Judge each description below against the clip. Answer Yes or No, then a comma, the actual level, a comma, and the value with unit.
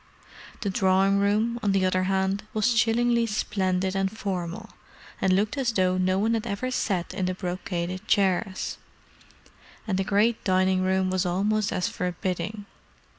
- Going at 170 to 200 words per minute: No, average, 155 wpm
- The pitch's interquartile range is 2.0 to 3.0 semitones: Yes, narrow, 2.5 semitones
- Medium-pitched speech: No, high, 195 Hz